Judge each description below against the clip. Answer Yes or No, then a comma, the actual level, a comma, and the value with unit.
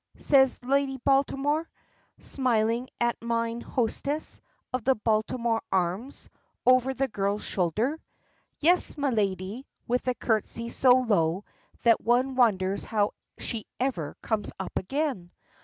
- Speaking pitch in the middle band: No, high, 235 Hz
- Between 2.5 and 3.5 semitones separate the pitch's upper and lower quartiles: No, average, 4.0 semitones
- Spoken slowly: Yes, slow, 125 wpm